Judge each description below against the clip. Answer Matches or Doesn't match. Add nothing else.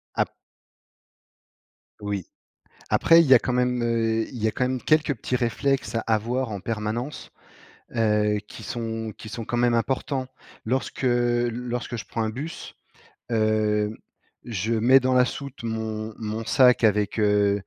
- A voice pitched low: Matches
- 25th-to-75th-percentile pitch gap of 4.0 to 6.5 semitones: Doesn't match